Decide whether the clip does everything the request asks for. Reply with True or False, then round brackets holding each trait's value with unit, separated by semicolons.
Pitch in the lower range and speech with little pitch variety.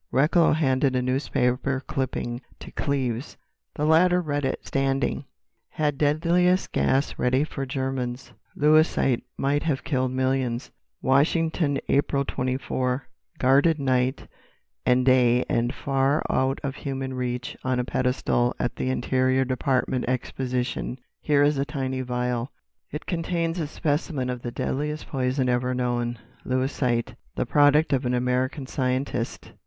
True (130 Hz; 2.3 semitones)